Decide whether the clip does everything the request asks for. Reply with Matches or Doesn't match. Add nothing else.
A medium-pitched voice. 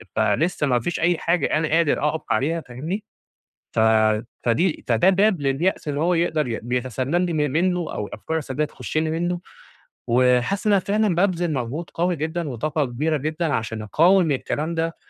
Matches